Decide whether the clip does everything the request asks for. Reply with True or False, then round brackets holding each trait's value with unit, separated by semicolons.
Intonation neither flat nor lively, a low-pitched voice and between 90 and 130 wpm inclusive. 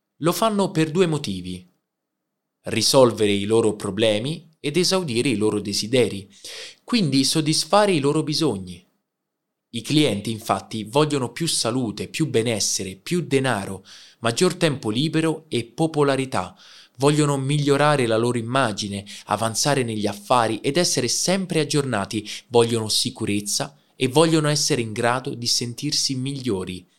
False (6.1 semitones; 130 Hz; 125 wpm)